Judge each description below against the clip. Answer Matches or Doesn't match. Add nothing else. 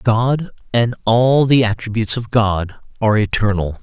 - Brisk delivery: Doesn't match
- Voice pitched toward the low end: Matches